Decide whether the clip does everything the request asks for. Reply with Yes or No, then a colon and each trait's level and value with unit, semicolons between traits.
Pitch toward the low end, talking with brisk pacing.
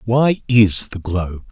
No: low, 105 Hz; average, 160 wpm